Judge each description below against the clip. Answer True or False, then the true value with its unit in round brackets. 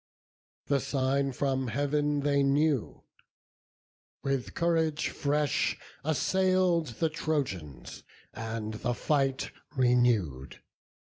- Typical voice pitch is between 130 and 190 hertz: True (140 Hz)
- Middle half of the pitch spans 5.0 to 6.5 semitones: False (3.6 semitones)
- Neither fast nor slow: False (85 wpm)